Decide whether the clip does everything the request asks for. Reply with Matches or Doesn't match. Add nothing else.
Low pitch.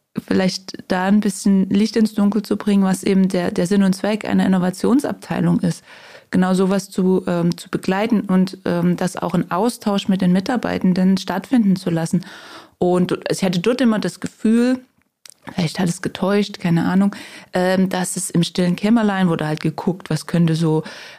Doesn't match